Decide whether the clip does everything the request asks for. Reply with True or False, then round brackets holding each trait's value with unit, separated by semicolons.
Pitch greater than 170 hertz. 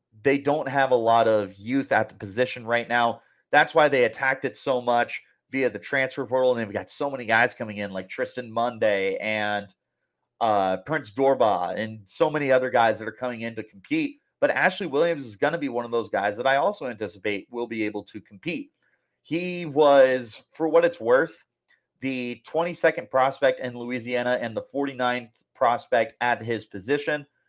False (125 Hz)